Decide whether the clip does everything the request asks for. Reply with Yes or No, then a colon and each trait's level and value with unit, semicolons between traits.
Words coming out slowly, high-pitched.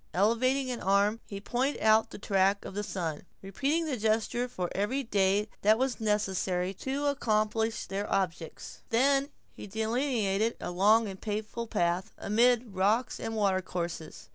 No: average, 155 wpm; high, 215 Hz